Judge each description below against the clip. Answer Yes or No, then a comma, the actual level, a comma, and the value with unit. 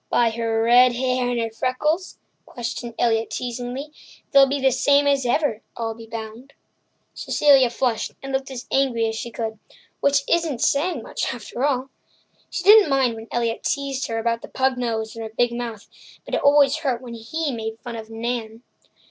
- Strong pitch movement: No, average, 3.1 semitones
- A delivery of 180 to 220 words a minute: Yes, average, 185 wpm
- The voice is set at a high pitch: Yes, high, 245 Hz